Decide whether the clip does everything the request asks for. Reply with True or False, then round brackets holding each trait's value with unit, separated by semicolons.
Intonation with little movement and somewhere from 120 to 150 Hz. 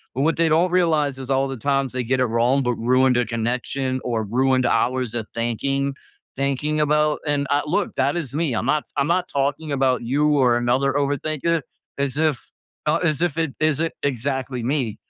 False (3.1 semitones; 135 Hz)